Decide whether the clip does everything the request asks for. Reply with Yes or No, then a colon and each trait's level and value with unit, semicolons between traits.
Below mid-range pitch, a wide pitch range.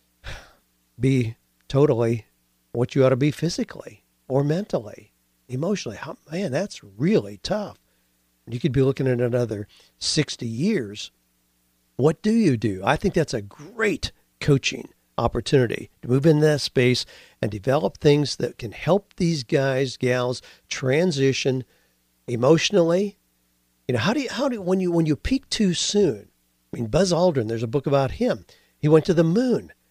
Yes: low, 130 Hz; wide, 8.2 semitones